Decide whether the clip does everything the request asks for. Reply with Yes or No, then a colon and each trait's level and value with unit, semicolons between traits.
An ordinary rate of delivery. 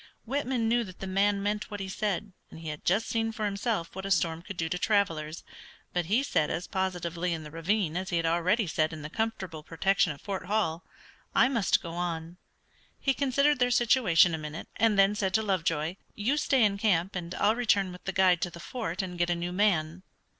No: fast, 225 wpm